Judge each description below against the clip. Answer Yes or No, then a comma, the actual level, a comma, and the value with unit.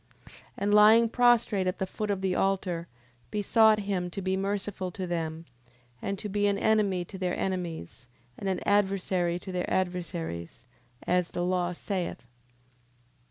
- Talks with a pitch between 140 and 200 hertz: Yes, high, 190 Hz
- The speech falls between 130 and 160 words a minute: Yes, average, 155 wpm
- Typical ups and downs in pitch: No, narrow, 2.3 semitones